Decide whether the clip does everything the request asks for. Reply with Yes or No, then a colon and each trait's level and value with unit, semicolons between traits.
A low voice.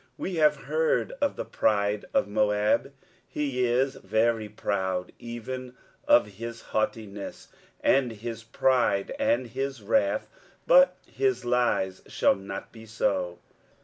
Yes: low, 115 Hz